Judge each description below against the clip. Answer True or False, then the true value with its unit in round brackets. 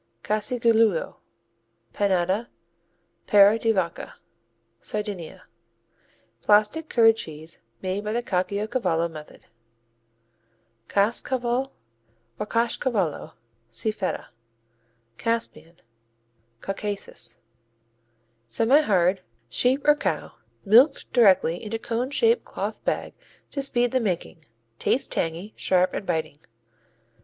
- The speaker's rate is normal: False (90 wpm)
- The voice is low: False (210 Hz)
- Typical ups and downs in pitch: True (4.6 semitones)